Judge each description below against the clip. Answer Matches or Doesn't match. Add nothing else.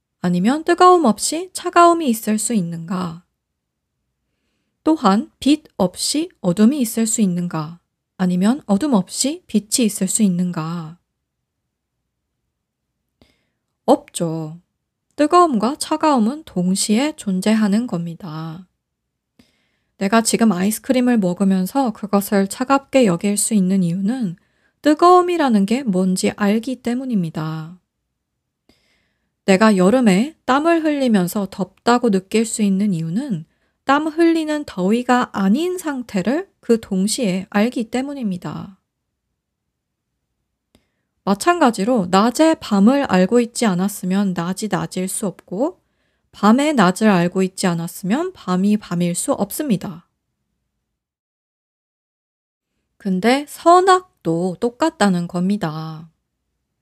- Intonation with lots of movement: Matches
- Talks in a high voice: Matches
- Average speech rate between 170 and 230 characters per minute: Matches